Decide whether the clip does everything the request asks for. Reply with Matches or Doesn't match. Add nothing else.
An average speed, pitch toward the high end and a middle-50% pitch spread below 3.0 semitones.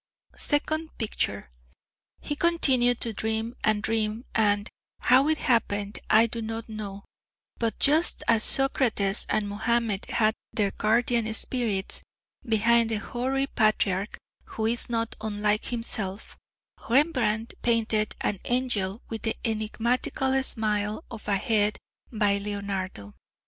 Doesn't match